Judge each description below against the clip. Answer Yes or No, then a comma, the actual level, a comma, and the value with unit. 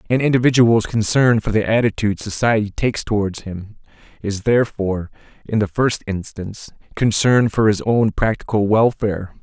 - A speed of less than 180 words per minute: Yes, average, 140 wpm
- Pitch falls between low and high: No, low, 110 Hz